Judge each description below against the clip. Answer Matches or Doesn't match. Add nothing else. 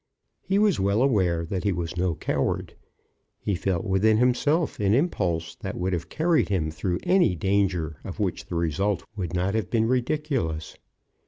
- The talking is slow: Doesn't match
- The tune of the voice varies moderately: Doesn't match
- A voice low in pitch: Matches